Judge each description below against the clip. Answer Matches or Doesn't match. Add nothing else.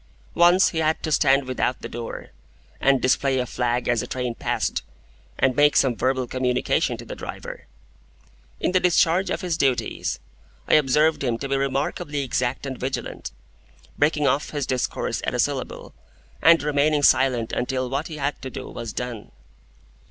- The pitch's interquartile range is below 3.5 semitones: Matches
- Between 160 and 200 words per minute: Matches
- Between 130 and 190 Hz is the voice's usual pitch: Matches